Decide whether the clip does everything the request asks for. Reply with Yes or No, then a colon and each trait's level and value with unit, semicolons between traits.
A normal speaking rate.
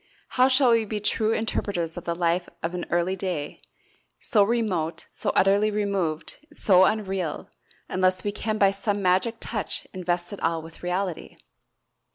Yes: average, 160 wpm